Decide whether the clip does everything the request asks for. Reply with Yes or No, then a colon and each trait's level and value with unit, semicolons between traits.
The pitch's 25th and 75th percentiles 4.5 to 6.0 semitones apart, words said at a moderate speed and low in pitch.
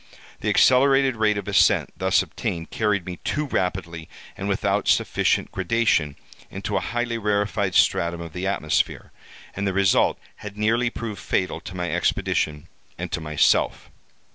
Yes: average, 4.9 semitones; average, 150 wpm; low, 100 Hz